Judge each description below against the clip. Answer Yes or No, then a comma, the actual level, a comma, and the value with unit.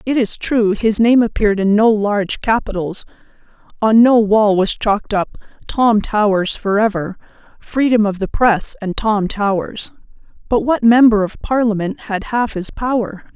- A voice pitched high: Yes, high, 215 Hz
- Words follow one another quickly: No, average, 155 wpm